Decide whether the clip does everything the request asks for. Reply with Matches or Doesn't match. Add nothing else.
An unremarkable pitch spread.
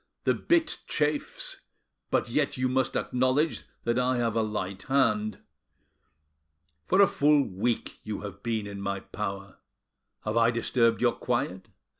Matches